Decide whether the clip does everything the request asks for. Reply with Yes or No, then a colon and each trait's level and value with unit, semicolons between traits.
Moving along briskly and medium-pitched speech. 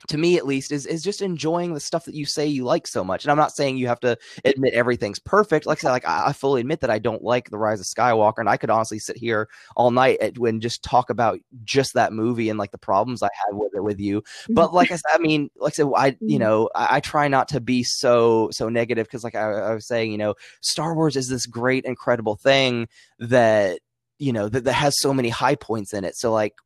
No: fast, 265 wpm; low, 125 Hz